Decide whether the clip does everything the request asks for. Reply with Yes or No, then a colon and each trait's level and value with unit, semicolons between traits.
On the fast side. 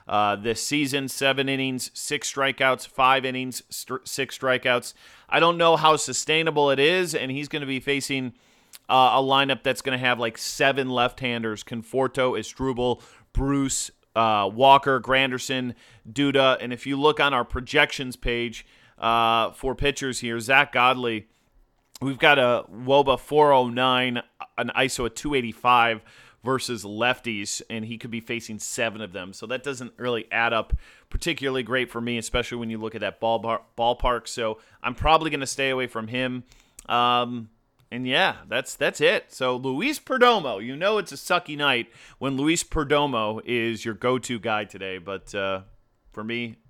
No: average, 165 wpm